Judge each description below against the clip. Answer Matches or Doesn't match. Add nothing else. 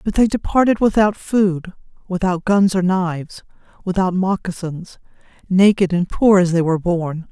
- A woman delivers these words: Matches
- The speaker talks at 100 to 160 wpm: Matches